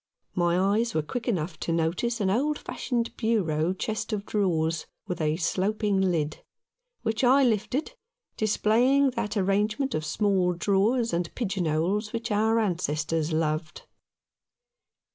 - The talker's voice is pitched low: No, high, 200 Hz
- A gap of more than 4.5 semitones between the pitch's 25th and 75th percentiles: Yes, average, 5.1 semitones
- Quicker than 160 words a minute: No, slow, 135 wpm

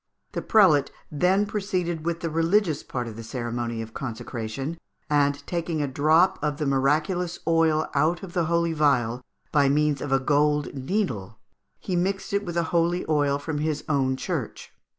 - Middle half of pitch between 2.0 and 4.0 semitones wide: Yes, average, 3.7 semitones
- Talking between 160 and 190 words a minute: Yes, average, 170 wpm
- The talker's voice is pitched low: No, medium, 150 Hz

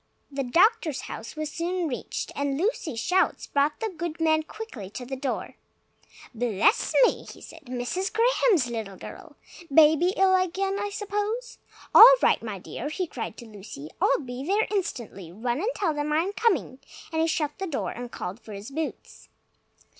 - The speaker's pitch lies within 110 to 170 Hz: No, very high, 310 Hz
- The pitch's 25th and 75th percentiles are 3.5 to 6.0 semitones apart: No, wide, 7.6 semitones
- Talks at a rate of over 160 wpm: Yes, average, 175 wpm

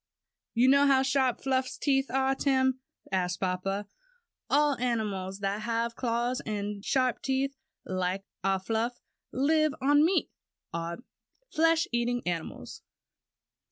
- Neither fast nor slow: No, slow, 125 wpm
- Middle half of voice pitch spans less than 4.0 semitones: No, average, 5.3 semitones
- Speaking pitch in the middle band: No, high, 245 Hz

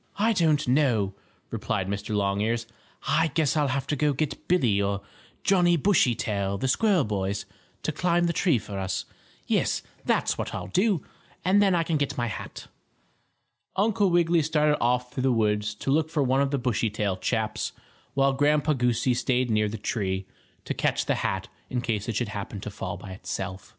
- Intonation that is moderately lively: No, wide, 7.0 semitones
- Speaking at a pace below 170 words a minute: No, average, 185 wpm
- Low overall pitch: Yes, low, 130 Hz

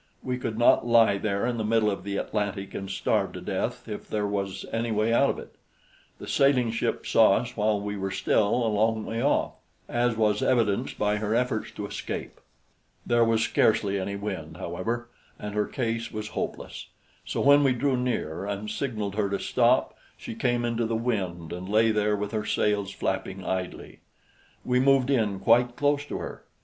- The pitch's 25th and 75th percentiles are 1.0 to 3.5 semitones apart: Yes, average, 2.7 semitones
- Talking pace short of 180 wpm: No, average, 190 wpm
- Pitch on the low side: Yes, low, 110 Hz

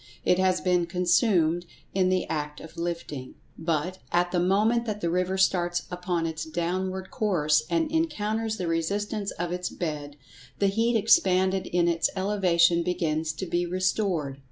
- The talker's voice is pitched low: No, medium, 180 Hz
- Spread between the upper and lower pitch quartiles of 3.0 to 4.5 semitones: No, narrow, 2.4 semitones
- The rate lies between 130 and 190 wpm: Yes, average, 155 wpm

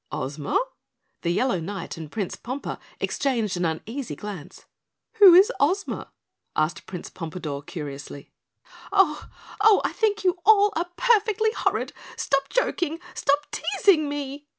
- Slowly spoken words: Yes, slow, 130 wpm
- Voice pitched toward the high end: Yes, very high, 280 Hz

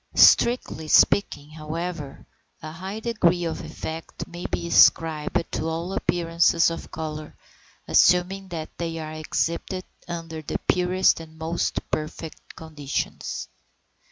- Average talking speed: No, slow, 120 wpm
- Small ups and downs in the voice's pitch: Yes, narrow, 2.1 semitones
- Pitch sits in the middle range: Yes, medium, 165 Hz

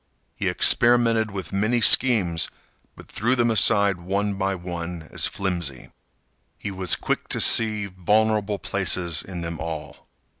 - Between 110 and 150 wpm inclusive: Yes, average, 140 wpm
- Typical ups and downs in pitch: Yes, average, 3.7 semitones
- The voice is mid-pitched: No, low, 100 Hz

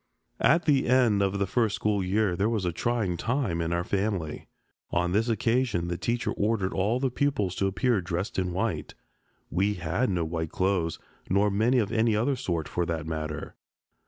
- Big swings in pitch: No, average, 4.8 semitones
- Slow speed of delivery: No, average, 190 wpm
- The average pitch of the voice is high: No, low, 100 Hz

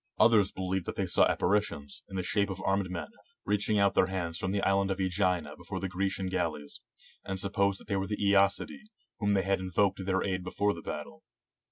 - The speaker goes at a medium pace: No, fast, 220 wpm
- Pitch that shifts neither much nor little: No, narrow, 1.3 semitones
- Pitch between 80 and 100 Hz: Yes, very low, 95 Hz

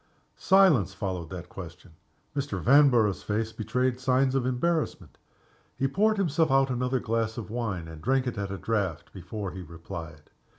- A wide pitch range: Yes, wide, 6.1 semitones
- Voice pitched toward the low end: Yes, low, 115 Hz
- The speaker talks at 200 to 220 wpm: No, average, 160 wpm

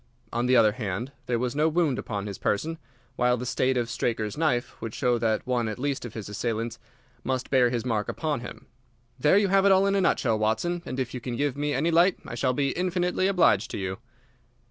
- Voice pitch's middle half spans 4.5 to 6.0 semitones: Yes, average, 5.3 semitones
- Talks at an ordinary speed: No, fast, 230 wpm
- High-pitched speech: No, low, 125 Hz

